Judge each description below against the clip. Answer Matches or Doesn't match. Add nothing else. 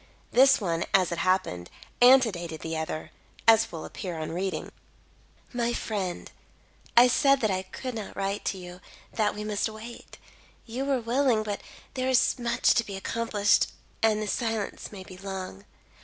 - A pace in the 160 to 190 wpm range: Matches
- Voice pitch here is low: Doesn't match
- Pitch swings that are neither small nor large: Matches